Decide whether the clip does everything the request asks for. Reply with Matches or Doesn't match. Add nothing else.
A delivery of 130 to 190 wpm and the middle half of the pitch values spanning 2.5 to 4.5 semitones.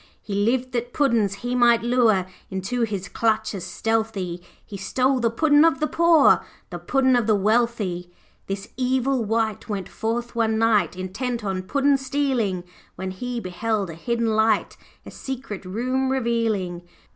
Matches